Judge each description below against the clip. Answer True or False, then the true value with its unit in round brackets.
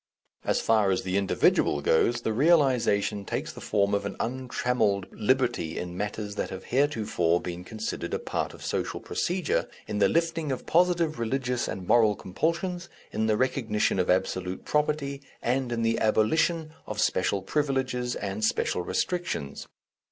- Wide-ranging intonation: True (5.7 semitones)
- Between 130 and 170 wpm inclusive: True (155 wpm)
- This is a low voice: True (115 Hz)